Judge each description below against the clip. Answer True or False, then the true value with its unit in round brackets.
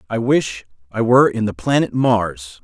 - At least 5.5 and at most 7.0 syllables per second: False (4.7 syllables/s)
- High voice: False (120 Hz)